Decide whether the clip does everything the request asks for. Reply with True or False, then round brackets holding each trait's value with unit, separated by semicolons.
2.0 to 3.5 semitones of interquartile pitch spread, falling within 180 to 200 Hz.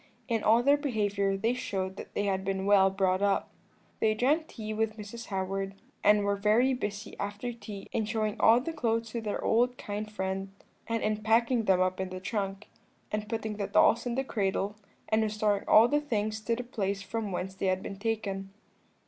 False (2.7 semitones; 210 Hz)